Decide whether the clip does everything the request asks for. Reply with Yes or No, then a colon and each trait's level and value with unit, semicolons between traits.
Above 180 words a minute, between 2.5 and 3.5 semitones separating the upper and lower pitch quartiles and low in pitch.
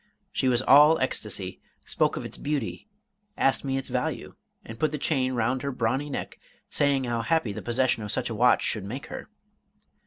Yes: average, 190 wpm; average, 3.1 semitones; low, 130 Hz